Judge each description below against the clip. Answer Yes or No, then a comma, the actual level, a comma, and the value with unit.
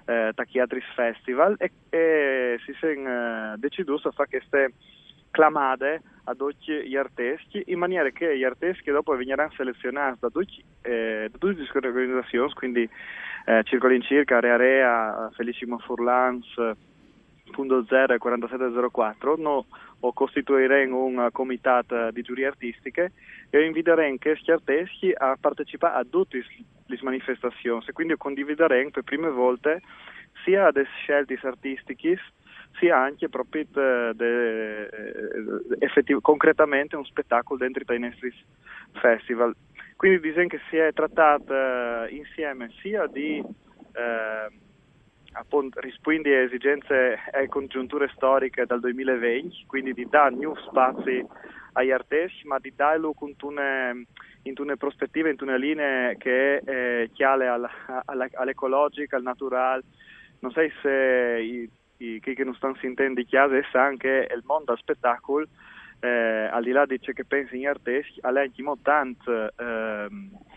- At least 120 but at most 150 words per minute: Yes, average, 130 wpm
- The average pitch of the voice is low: Yes, low, 130 Hz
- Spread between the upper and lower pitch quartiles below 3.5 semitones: Yes, average, 2.9 semitones